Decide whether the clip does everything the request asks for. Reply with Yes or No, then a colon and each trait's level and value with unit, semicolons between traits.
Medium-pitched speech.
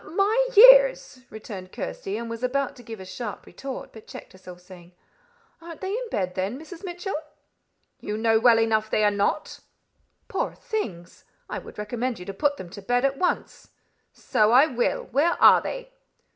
No: high, 240 Hz